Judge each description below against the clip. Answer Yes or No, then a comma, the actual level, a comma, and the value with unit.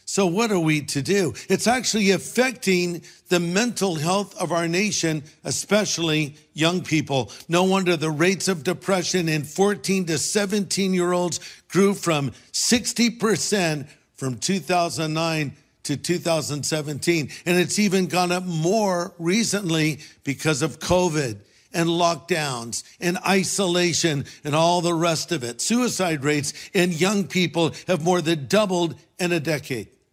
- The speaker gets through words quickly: No, slow, 135 wpm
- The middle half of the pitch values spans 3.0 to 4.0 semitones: Yes, average, 3.5 semitones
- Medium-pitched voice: Yes, medium, 175 Hz